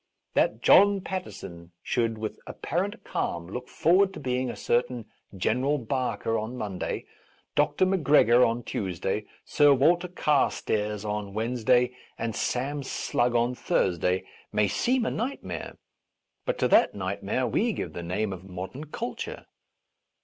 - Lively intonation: Yes, wide, 5.8 semitones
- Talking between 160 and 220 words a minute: No, average, 145 wpm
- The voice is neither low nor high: No, low, 120 Hz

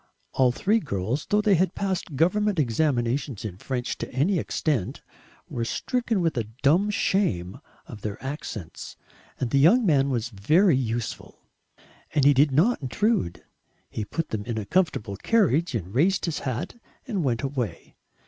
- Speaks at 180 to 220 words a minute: No, average, 160 wpm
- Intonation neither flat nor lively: No, wide, 7.9 semitones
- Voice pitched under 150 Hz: Yes, medium, 140 Hz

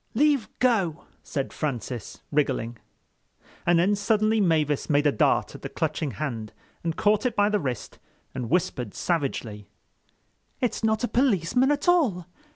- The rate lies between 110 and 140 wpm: No, average, 150 wpm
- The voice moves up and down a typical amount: No, wide, 7.9 semitones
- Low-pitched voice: No, medium, 170 Hz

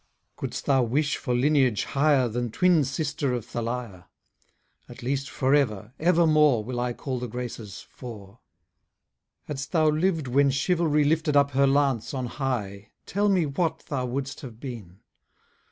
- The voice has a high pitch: No, low, 135 Hz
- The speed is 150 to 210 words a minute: Yes, average, 155 wpm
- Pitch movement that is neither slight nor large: Yes, average, 3.7 semitones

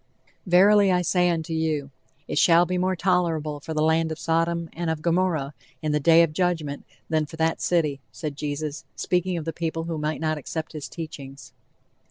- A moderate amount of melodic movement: No, narrow, 2.2 semitones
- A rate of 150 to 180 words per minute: No, average, 195 wpm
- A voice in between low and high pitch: Yes, medium, 160 Hz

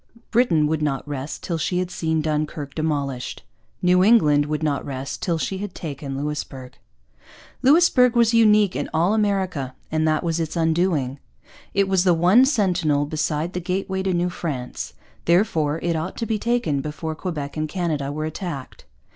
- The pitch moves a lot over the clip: No, average, 4.2 semitones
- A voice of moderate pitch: Yes, medium, 160 Hz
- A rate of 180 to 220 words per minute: No, average, 170 wpm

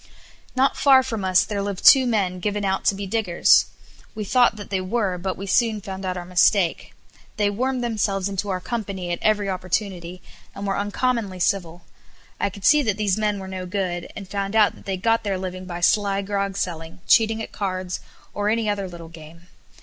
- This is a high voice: Yes, high, 195 Hz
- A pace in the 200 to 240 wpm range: Yes, fast, 205 wpm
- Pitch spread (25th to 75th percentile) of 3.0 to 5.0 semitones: No, narrow, 2.5 semitones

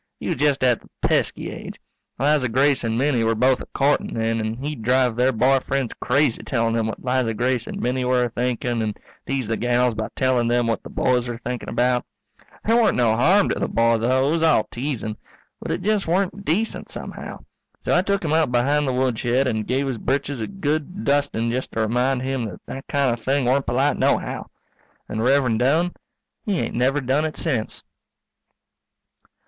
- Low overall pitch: Yes, low, 130 Hz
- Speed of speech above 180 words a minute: Yes, fast, 205 wpm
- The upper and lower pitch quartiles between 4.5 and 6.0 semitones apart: No, average, 3.2 semitones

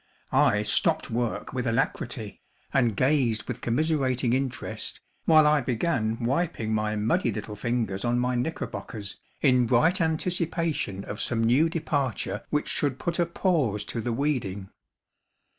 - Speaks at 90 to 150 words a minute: Yes, average, 140 wpm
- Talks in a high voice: No, low, 125 Hz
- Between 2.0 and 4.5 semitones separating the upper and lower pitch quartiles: No, wide, 5.4 semitones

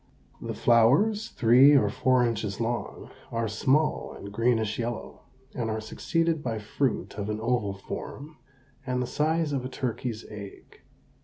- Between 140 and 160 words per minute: Yes, average, 150 wpm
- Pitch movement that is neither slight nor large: Yes, average, 3.7 semitones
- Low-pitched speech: Yes, low, 120 Hz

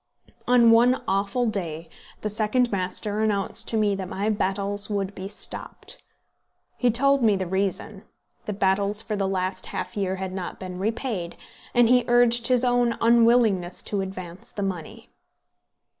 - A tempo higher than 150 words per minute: Yes, average, 160 wpm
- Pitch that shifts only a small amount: No, average, 3.5 semitones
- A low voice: No, high, 205 Hz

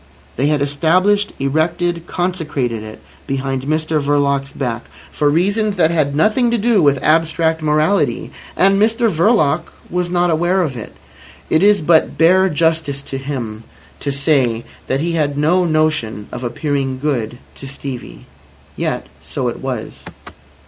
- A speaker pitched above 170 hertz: No, medium, 155 Hz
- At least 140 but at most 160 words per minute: Yes, average, 150 wpm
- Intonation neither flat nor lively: Yes, average, 4.2 semitones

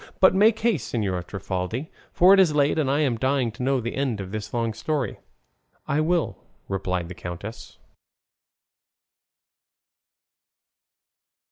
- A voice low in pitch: Yes, low, 125 Hz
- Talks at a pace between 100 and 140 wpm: Yes, slow, 135 wpm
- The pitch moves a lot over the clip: Yes, wide, 7.1 semitones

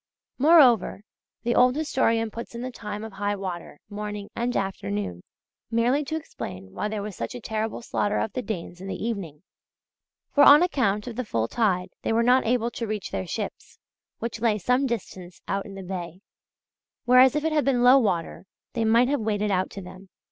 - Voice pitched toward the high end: Yes, high, 220 Hz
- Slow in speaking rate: No, average, 195 wpm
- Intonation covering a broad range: No, average, 4.3 semitones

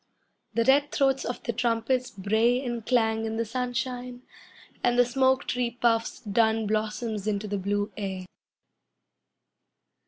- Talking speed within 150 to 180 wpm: No, slow, 135 wpm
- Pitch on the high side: Yes, high, 230 Hz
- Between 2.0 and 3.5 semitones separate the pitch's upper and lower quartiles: Yes, narrow, 2.5 semitones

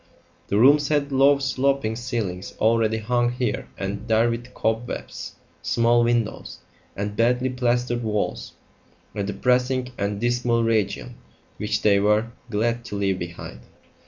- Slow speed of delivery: Yes, slow, 130 wpm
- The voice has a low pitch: Yes, low, 115 Hz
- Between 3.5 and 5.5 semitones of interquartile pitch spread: No, average, 2.8 semitones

